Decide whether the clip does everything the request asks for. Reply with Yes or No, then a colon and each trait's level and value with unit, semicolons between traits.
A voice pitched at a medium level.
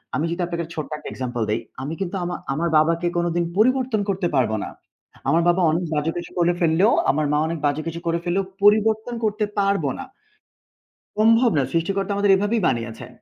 Yes: medium, 175 Hz